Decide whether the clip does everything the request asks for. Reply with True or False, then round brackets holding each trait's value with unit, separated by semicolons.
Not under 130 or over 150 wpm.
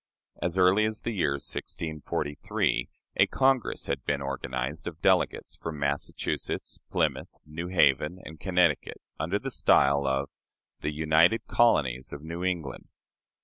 True (135 wpm)